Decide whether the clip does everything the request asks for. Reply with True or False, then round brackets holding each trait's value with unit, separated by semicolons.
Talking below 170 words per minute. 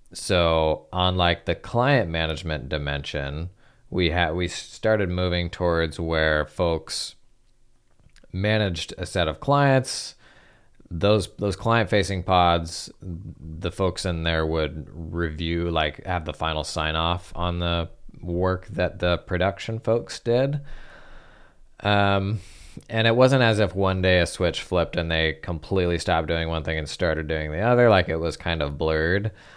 True (150 wpm)